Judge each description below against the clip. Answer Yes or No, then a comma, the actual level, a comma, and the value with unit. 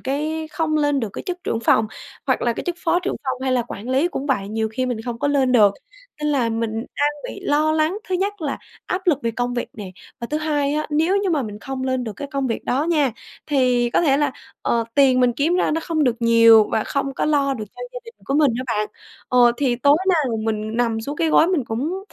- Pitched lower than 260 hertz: No, very high, 270 Hz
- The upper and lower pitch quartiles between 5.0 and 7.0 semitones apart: No, average, 4.6 semitones